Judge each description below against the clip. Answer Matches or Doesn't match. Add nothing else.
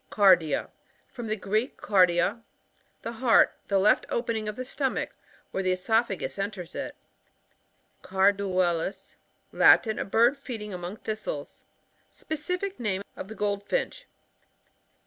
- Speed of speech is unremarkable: Doesn't match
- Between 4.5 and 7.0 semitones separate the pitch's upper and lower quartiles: Doesn't match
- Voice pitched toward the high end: Matches